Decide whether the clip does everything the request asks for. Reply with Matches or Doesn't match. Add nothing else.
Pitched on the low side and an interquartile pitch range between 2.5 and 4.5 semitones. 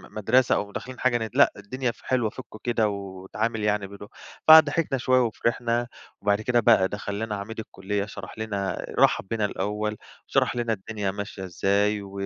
Matches